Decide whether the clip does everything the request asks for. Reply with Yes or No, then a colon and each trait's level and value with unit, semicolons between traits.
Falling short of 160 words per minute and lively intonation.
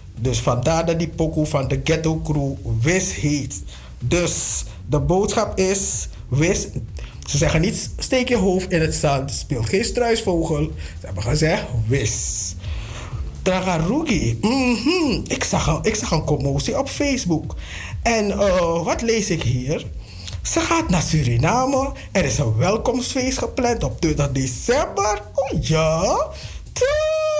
Yes: average, 140 wpm; wide, 8.7 semitones